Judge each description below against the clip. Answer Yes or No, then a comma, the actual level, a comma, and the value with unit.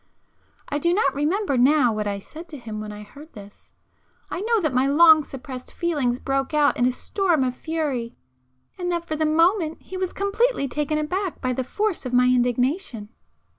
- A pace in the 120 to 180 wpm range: No, average, 190 wpm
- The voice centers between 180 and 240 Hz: No, very high, 290 Hz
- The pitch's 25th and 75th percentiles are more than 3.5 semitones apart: Yes, wide, 5.4 semitones